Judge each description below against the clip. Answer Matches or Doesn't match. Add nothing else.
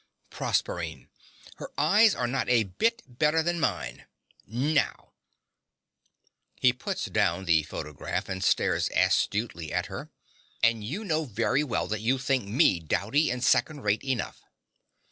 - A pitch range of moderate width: Doesn't match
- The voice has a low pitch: Matches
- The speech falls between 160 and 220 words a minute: Doesn't match